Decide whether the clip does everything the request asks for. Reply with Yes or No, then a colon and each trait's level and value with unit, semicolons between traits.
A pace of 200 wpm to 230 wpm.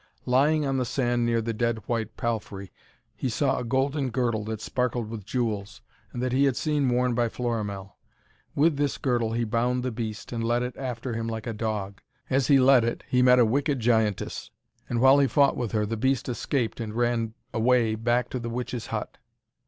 Yes: fast, 205 wpm